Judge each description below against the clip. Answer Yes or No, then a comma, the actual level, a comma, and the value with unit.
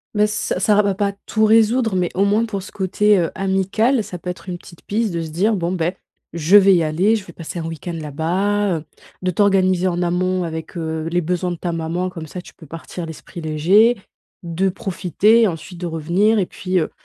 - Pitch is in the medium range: Yes, medium, 180 Hz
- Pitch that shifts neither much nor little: Yes, average, 3.2 semitones